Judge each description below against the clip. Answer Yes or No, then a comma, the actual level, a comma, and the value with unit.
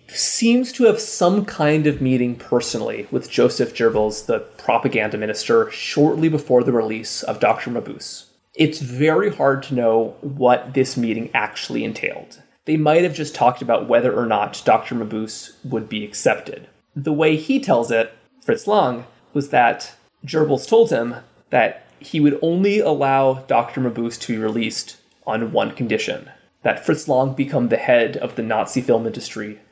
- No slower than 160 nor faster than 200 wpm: Yes, average, 165 wpm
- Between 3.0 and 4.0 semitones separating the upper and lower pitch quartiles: No, average, 5.1 semitones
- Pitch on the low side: Yes, low, 130 Hz